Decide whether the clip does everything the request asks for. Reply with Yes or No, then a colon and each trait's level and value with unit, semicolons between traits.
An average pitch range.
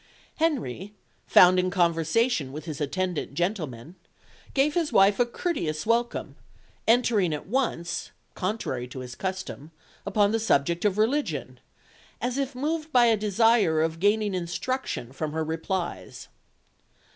No: wide, 6.6 semitones